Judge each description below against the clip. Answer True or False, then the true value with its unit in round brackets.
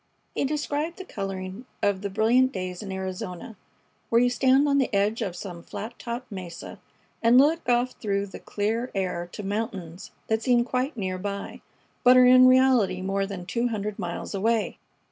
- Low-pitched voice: False (215 Hz)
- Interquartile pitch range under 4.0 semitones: False (4.7 semitones)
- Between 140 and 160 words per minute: False (180 wpm)